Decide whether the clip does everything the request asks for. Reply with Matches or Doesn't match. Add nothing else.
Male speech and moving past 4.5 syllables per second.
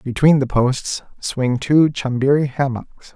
Doesn't match